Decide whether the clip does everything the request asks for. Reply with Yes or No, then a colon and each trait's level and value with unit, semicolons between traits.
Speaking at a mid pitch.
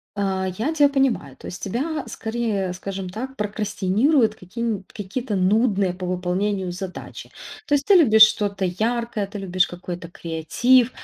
No: high, 205 Hz